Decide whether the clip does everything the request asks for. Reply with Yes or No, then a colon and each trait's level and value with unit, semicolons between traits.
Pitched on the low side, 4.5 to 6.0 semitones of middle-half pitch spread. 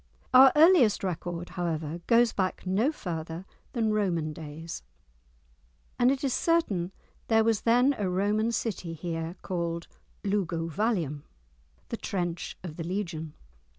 No: medium, 185 Hz; average, 5.2 semitones